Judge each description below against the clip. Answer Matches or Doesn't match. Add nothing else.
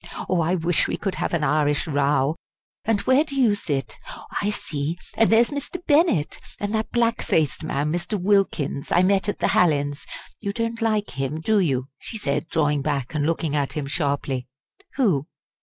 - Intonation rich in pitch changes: Matches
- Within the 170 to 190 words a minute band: Matches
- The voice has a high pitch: Doesn't match